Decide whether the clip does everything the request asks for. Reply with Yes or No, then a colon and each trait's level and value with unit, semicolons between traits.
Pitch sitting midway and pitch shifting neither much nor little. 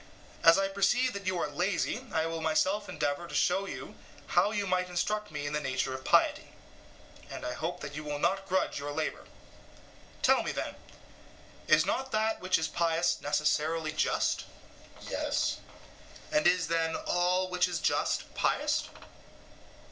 Yes: medium, 170 Hz; average, 3.9 semitones